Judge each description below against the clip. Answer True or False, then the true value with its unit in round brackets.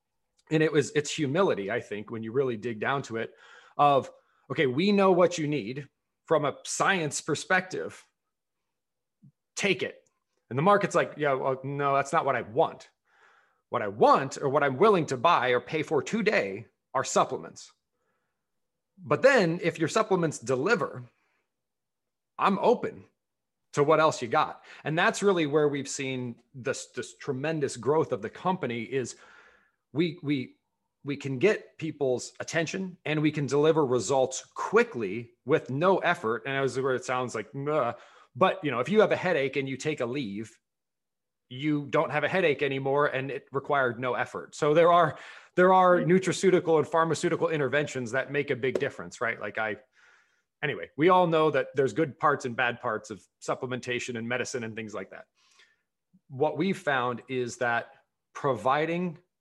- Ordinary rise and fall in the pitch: True (4.3 semitones)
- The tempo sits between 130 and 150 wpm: False (170 wpm)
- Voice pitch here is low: False (145 Hz)